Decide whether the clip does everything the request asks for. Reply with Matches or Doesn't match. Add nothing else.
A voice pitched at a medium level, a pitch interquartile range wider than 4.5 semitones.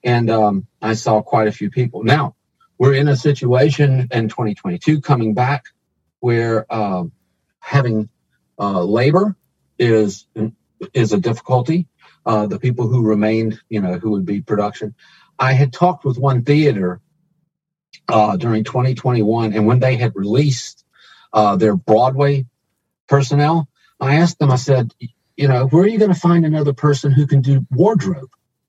Doesn't match